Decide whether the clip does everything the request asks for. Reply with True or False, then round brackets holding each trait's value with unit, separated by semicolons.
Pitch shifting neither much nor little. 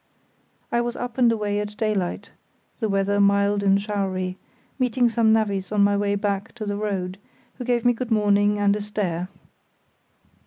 False (1.9 semitones)